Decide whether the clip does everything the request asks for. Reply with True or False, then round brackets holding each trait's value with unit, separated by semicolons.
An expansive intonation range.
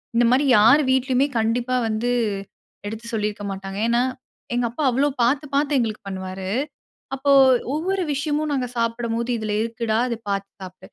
False (3.8 semitones)